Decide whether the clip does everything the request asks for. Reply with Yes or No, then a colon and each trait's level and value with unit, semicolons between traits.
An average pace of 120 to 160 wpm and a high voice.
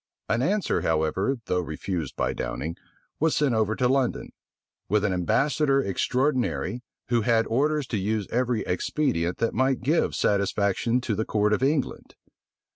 No: average, 150 wpm; low, 115 Hz